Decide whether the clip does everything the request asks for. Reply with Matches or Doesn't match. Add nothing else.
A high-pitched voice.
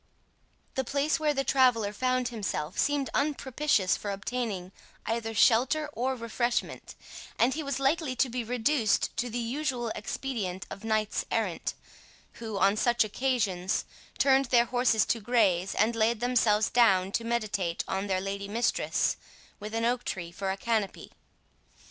Matches